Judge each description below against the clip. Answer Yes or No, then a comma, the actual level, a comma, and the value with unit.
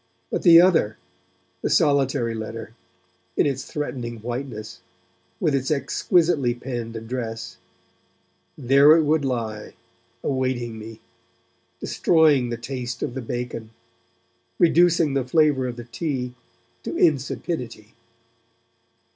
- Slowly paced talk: Yes, slow, 110 wpm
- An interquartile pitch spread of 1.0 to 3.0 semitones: No, average, 3.8 semitones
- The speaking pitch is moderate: No, low, 125 Hz